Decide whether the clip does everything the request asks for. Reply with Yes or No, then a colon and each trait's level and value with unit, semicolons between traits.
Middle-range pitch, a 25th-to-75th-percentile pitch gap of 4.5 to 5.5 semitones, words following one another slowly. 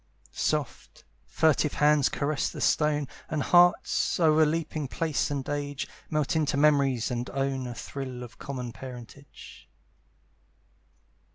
No: medium, 145 Hz; narrow, 2.4 semitones; slow, 115 wpm